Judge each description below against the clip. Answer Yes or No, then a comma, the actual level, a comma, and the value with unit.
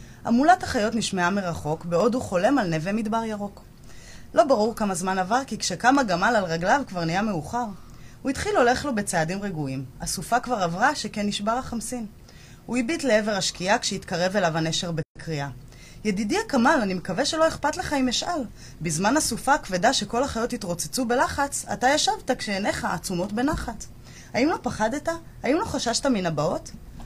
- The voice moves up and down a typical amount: No, wide, 6.1 semitones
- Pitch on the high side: Yes, high, 215 Hz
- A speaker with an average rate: No, fast, 160 wpm